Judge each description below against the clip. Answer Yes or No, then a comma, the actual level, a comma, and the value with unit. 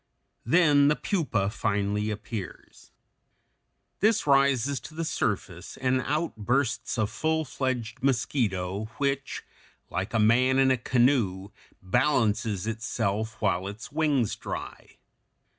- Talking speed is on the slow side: Yes, slow, 115 wpm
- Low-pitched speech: Yes, low, 120 Hz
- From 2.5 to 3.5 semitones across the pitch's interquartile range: No, average, 5.1 semitones